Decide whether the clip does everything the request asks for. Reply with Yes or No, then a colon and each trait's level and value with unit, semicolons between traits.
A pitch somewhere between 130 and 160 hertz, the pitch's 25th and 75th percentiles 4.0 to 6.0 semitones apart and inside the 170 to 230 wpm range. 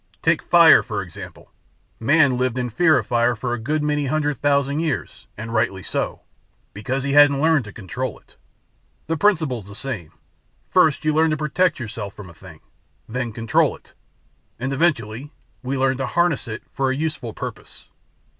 Yes: low, 135 Hz; average, 4.7 semitones; average, 175 wpm